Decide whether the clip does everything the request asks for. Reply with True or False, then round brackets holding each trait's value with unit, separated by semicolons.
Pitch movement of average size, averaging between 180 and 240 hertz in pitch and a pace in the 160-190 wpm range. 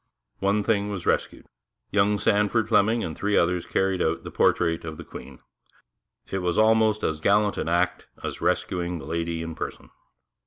False (3.7 semitones; 95 Hz; 170 wpm)